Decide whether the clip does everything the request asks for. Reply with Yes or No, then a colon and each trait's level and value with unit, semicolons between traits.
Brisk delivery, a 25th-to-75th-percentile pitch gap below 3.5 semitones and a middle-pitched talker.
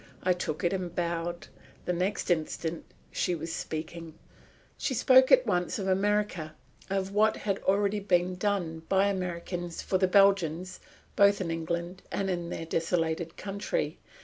No: average, 150 wpm; average, 2.8 semitones; medium, 180 Hz